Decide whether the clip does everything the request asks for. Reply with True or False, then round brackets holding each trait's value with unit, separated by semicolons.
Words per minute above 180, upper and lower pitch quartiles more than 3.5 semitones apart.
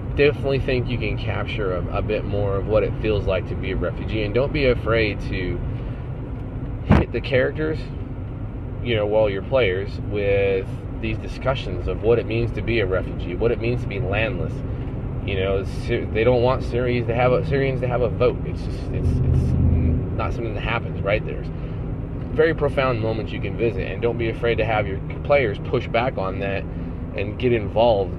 True (200 wpm; 4.0 semitones)